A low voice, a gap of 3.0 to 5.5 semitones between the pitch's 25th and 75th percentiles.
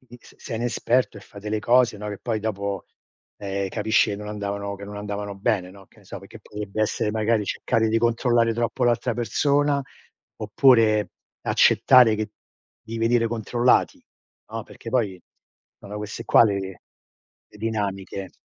No: low, 110 Hz; narrow, 2.5 semitones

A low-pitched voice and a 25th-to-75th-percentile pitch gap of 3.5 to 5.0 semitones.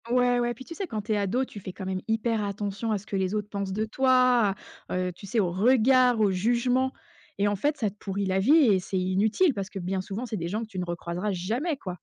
No: high, 210 Hz; average, 4.2 semitones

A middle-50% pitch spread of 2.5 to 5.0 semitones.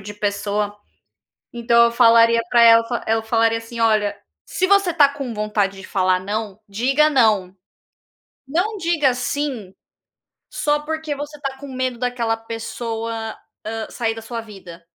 Yes: average, 4.0 semitones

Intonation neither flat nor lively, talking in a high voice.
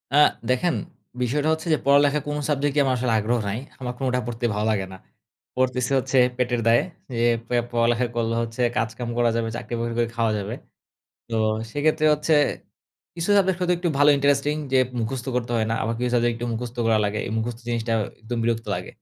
No: average, 3.5 semitones; low, 120 Hz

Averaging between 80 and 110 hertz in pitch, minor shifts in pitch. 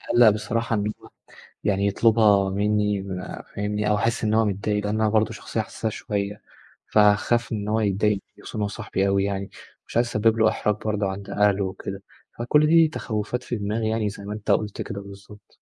Yes: low, 105 Hz; narrow, 1.6 semitones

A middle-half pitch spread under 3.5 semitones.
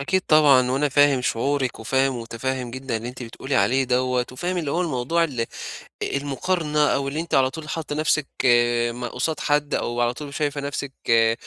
Yes: average, 3.1 semitones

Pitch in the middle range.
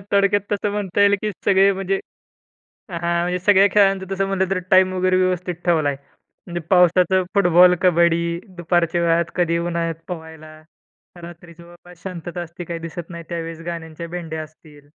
Yes: medium, 175 Hz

